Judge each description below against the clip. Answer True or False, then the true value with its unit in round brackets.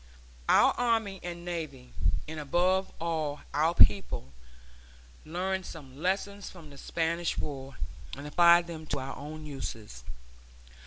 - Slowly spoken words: True (125 wpm)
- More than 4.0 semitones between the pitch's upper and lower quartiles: False (3.6 semitones)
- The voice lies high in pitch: False (160 Hz)